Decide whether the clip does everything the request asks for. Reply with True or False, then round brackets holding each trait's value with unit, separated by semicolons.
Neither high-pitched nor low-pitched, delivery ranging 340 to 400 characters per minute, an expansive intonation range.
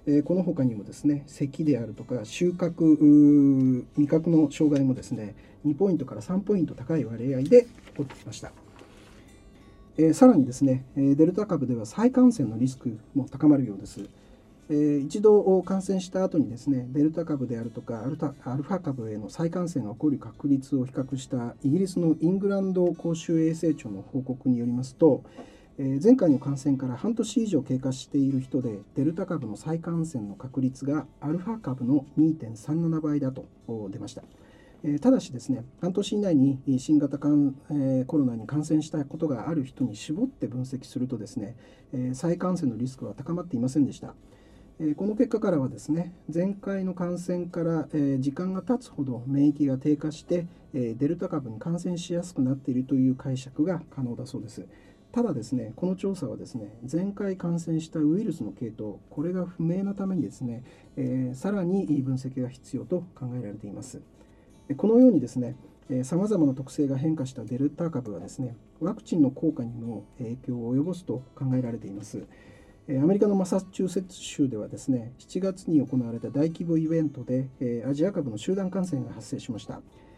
False (145 Hz; 355 characters per minute; 4.9 semitones)